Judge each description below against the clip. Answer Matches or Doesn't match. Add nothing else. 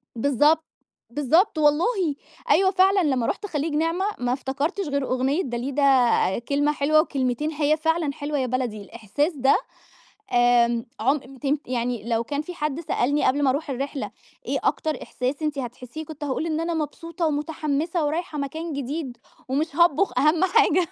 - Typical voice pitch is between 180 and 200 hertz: Doesn't match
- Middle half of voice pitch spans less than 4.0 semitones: Matches